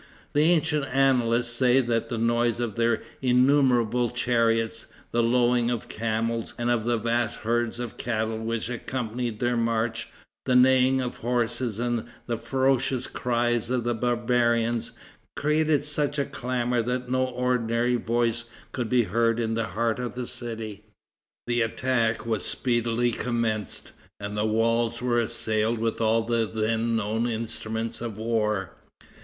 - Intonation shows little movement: Yes, narrow, 1.5 semitones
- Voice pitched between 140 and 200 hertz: No, low, 120 Hz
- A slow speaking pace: No, average, 150 wpm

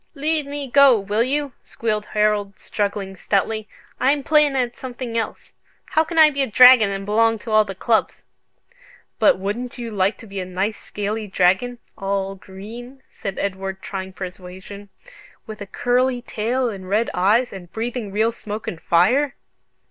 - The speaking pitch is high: Yes, high, 215 Hz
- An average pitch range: Yes, average, 4.1 semitones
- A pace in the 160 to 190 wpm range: Yes, average, 165 wpm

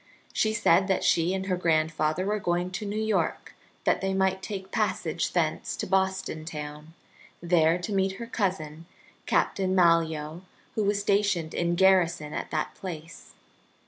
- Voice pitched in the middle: Yes, medium, 180 Hz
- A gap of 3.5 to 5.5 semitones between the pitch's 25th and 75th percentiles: No, average, 3.0 semitones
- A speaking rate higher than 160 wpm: No, average, 155 wpm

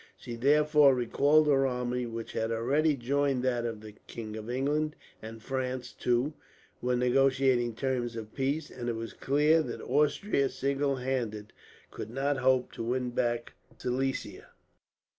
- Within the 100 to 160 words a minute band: Yes, average, 145 wpm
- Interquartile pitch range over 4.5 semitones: No, average, 2.7 semitones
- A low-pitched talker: Yes, low, 130 Hz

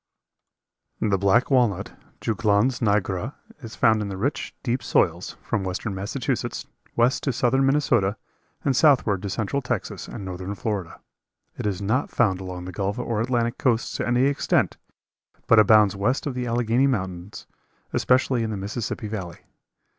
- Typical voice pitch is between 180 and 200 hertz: No, low, 110 Hz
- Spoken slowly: No, average, 155 wpm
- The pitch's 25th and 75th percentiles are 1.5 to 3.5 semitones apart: No, average, 4.1 semitones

